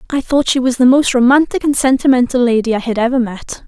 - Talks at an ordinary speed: No, fast, 230 wpm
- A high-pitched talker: Yes, very high, 255 Hz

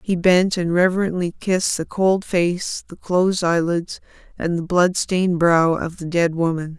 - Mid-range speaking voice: Yes, medium, 175 Hz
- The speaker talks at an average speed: Yes, average, 175 wpm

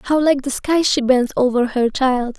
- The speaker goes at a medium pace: No, fast, 225 wpm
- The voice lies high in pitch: Yes, very high, 260 Hz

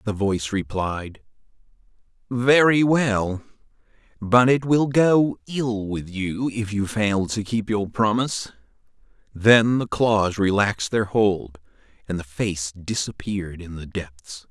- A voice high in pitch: No, low, 105 Hz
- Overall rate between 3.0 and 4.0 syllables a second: Yes, 3.8 syllables/s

